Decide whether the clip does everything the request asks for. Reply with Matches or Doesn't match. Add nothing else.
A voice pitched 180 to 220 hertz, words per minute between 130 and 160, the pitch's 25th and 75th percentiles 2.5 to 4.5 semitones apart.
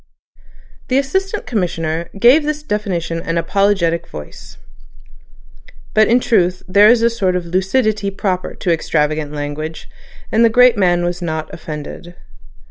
Doesn't match